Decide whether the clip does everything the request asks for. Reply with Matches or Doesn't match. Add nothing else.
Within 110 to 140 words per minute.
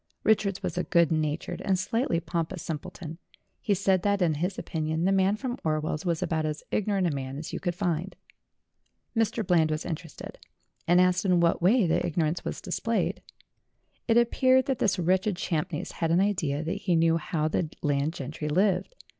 Doesn't match